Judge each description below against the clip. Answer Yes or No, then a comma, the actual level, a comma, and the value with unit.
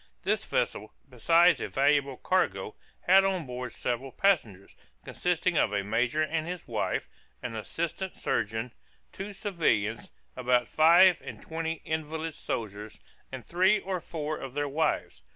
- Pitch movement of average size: No, wide, 6.2 semitones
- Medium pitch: Yes, medium, 150 Hz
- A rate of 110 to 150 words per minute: Yes, average, 140 wpm